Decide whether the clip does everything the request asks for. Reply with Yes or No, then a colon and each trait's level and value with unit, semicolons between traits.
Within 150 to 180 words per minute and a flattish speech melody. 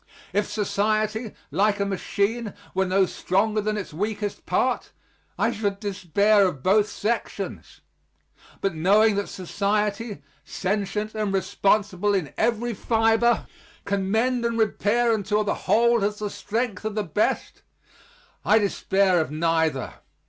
No: slow, 135 wpm; narrow, 1.9 semitones